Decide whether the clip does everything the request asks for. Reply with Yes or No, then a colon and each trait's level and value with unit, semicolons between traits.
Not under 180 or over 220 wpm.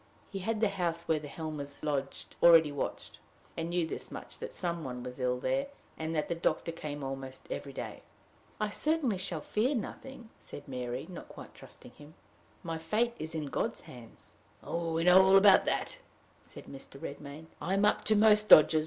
Yes: average, 185 wpm